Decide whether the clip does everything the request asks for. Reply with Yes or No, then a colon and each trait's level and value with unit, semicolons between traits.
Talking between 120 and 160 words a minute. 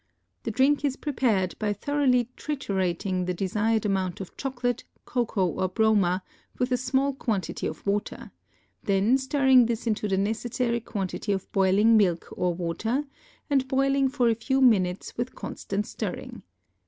Yes: average, 150 wpm